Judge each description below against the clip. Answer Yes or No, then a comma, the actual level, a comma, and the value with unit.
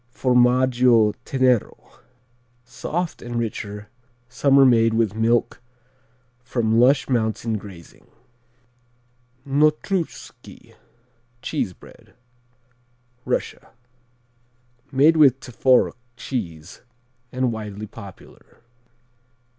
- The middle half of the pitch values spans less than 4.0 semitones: Yes, average, 2.9 semitones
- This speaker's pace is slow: Yes, slow, 75 wpm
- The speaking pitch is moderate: No, low, 120 Hz